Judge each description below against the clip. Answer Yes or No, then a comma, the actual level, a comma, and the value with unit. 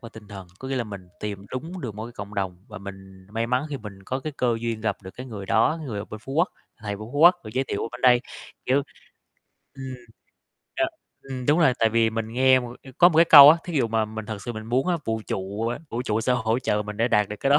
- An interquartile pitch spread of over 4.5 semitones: No, average, 3.8 semitones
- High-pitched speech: No, low, 115 Hz